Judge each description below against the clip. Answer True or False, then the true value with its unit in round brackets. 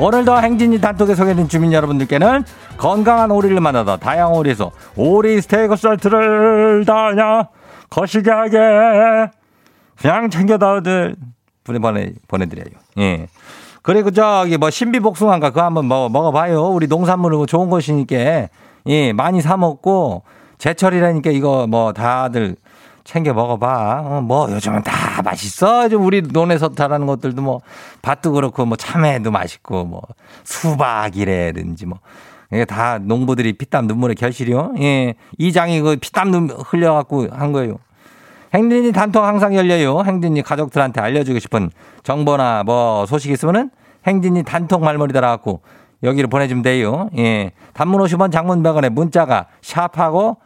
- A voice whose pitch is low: False (155 Hz)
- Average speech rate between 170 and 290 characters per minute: False (320 characters per minute)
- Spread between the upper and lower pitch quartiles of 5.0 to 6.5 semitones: False (7.5 semitones)